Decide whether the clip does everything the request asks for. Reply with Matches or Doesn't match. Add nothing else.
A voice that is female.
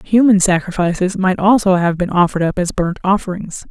Matches